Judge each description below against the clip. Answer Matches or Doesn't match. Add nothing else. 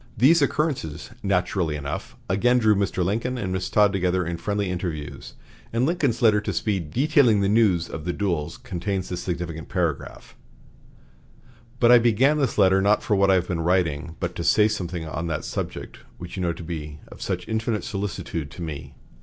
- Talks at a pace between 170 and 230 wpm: Matches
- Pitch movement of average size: Matches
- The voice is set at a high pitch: Doesn't match